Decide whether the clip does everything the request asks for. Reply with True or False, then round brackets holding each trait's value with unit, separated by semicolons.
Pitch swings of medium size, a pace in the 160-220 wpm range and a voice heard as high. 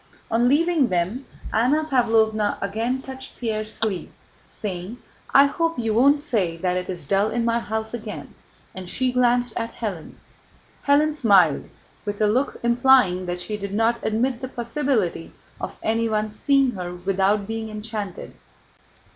False (4.0 semitones; 150 wpm; 220 Hz)